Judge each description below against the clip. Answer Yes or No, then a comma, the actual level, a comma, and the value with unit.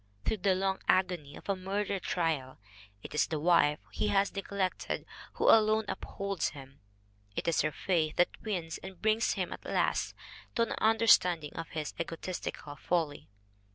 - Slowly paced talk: No, average, 165 wpm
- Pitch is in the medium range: Yes, medium, 180 Hz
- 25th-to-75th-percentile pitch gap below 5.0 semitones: Yes, average, 4.1 semitones